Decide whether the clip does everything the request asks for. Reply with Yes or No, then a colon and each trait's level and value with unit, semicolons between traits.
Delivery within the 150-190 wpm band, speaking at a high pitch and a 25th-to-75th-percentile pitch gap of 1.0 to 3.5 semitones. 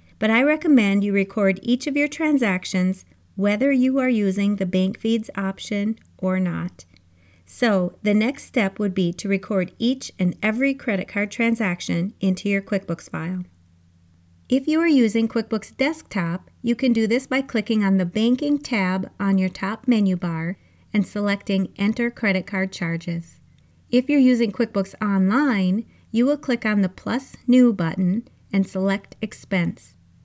No: average, 160 wpm; high, 205 Hz; average, 4.1 semitones